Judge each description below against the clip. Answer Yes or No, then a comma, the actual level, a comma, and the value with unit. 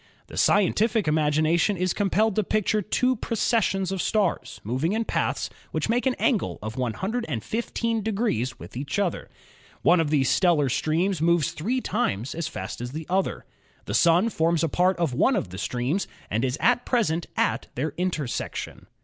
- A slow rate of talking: No, average, 170 wpm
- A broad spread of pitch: Yes, wide, 6.2 semitones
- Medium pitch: Yes, medium, 175 Hz